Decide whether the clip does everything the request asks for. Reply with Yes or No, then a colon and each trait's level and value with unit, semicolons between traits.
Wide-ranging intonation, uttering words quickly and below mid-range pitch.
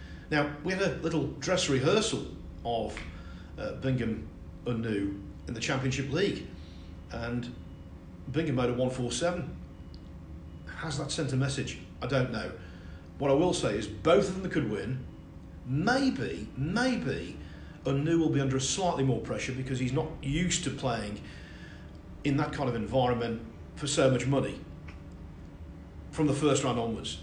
No: wide, 8.2 semitones; average, 150 wpm; low, 120 Hz